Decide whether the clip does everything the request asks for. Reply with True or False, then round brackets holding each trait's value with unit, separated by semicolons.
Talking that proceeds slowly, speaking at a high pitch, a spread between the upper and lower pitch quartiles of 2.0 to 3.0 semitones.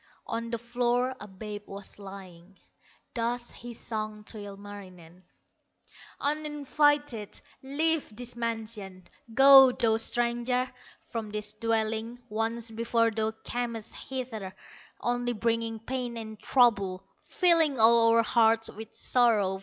True (115 wpm; 230 Hz; 2.4 semitones)